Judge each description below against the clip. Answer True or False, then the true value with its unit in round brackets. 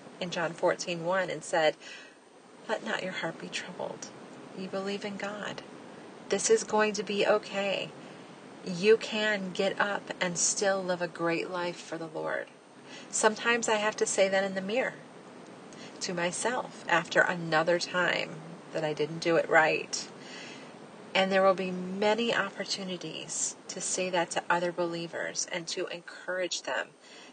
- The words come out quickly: False (155 wpm)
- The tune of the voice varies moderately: True (3.1 semitones)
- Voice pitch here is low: False (190 Hz)